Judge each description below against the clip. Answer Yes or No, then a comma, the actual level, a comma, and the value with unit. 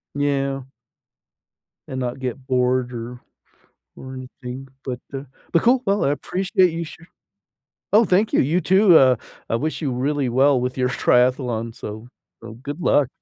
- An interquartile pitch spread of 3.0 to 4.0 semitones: Yes, average, 3.7 semitones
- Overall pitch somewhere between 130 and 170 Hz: Yes, low, 135 Hz